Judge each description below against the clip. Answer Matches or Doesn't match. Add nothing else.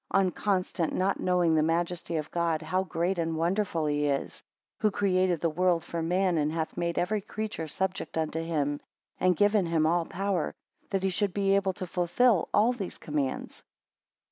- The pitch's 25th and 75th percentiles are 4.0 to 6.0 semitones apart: Doesn't match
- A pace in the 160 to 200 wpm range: Matches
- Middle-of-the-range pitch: Matches